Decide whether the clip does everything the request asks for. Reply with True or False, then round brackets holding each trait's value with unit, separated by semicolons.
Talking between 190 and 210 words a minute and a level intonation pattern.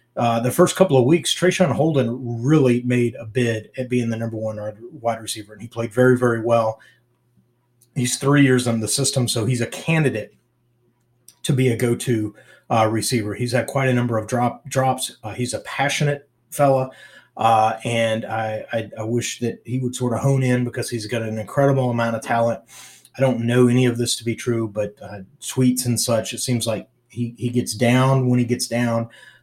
True (205 wpm; 2.1 semitones)